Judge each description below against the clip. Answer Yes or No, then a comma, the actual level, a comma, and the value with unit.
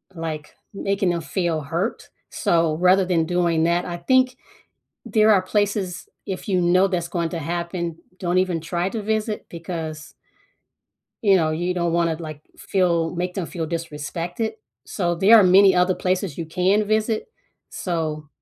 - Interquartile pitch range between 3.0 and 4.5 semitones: No, narrow, 2.5 semitones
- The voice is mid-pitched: Yes, medium, 175 Hz